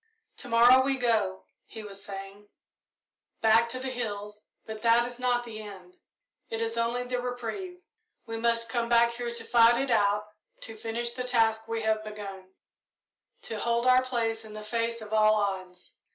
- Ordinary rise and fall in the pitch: No, narrow, 2.1 semitones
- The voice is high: Yes, high, 230 Hz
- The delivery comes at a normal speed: Yes, average, 180 wpm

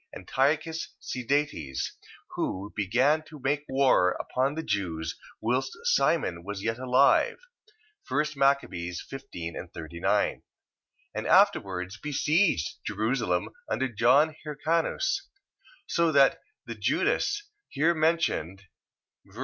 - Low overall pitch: Yes, low, 130 Hz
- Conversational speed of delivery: No, slow, 100 wpm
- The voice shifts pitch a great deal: Yes, wide, 7.7 semitones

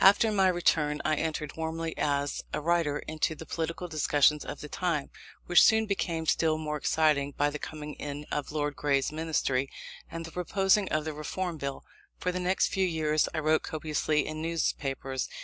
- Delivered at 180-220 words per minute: Yes, average, 185 wpm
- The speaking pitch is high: No, medium, 155 Hz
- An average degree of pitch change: No, narrow, 2.2 semitones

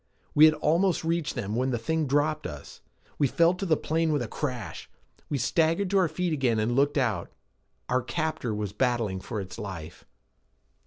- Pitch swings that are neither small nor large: No, wide, 6.0 semitones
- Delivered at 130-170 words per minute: No, average, 190 wpm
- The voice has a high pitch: No, medium, 140 Hz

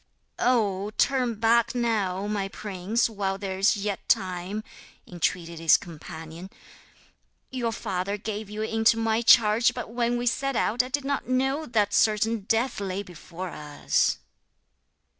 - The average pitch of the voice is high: Yes, high, 210 Hz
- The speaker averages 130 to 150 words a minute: Yes, average, 140 wpm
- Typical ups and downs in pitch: Yes, average, 3.7 semitones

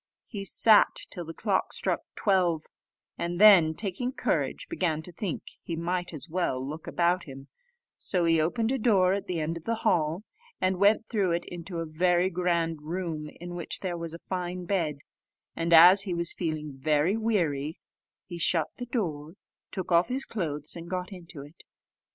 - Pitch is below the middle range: No, medium, 175 Hz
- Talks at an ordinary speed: Yes, average, 180 wpm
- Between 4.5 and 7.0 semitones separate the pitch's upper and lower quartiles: No, average, 2.8 semitones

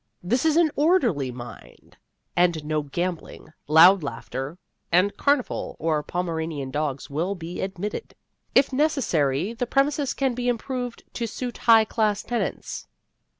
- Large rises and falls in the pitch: Yes, wide, 7.9 semitones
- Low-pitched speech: No, high, 190 Hz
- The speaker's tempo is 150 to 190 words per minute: No, slow, 135 wpm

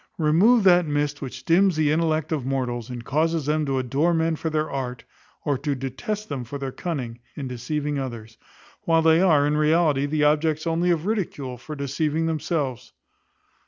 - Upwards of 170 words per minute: Yes, average, 180 wpm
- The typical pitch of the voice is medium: Yes, medium, 150 Hz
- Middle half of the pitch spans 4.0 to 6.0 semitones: No, average, 3.3 semitones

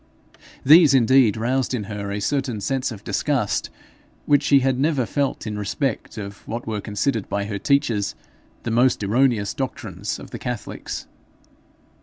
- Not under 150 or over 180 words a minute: Yes, average, 155 wpm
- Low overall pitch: Yes, low, 120 Hz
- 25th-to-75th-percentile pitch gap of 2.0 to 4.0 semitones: No, average, 4.5 semitones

